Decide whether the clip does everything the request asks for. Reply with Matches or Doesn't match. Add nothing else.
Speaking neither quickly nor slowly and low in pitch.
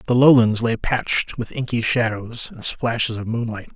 Matches